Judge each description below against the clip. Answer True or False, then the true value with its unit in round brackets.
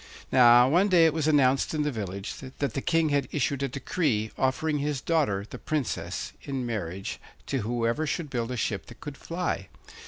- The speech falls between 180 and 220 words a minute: True (190 wpm)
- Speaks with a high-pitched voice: False (135 Hz)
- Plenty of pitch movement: False (4.5 semitones)